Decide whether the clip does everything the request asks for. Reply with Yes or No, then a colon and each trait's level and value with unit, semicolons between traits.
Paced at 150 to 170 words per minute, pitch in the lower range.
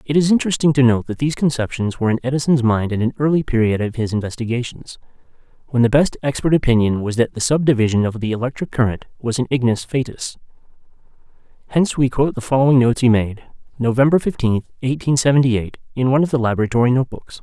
No: average, 195 wpm; low, 125 Hz